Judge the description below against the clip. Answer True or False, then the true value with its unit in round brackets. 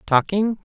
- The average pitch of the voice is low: False (190 Hz)